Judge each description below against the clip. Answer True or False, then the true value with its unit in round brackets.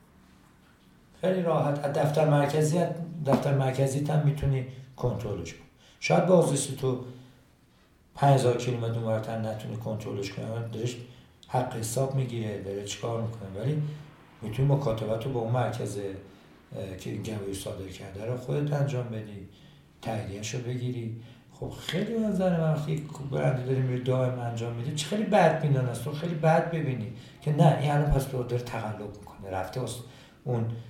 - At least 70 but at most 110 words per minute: False (150 wpm)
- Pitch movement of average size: True (4.4 semitones)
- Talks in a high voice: False (125 Hz)